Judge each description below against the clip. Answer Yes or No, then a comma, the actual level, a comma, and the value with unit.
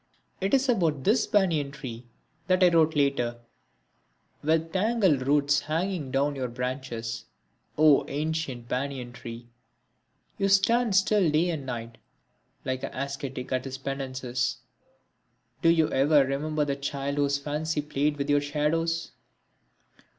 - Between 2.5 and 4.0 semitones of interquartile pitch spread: Yes, average, 3.6 semitones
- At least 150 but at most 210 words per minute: No, slow, 135 wpm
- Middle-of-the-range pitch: Yes, medium, 145 Hz